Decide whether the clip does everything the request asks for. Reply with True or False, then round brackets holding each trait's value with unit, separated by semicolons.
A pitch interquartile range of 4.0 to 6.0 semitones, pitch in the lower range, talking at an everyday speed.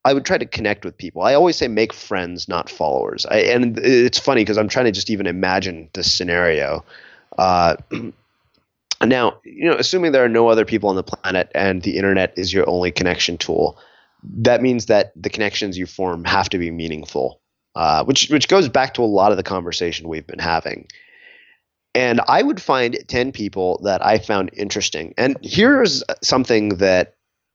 True (4.3 semitones; 100 Hz; 190 wpm)